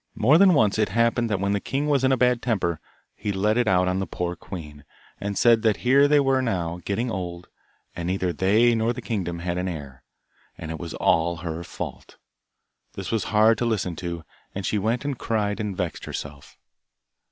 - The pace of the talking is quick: Yes, fast, 210 wpm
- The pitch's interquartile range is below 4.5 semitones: No, average, 5.1 semitones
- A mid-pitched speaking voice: No, low, 100 Hz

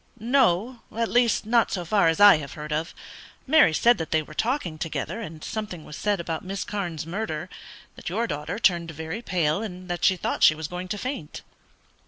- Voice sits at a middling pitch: Yes, medium, 180 Hz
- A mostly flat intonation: No, average, 5.3 semitones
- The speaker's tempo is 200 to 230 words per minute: Yes, fast, 205 wpm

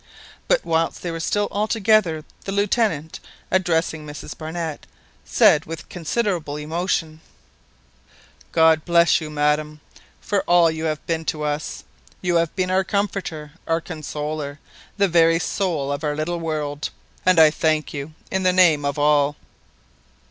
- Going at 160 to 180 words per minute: No, average, 145 wpm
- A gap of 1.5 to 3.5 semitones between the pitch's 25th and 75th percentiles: Yes, average, 3.1 semitones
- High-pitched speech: No, medium, 160 Hz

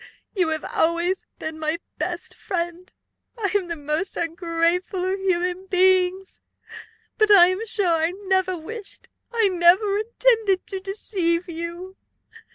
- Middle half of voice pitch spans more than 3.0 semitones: No, narrow, 2.4 semitones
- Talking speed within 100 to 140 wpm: Yes, slow, 135 wpm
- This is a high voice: Yes, very high, 370 Hz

